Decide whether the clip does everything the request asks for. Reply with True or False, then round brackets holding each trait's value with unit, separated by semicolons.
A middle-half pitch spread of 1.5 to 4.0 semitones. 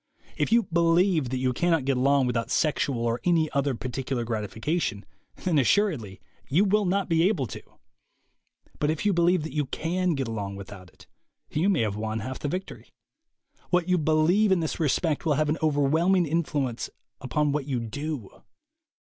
False (5.3 semitones)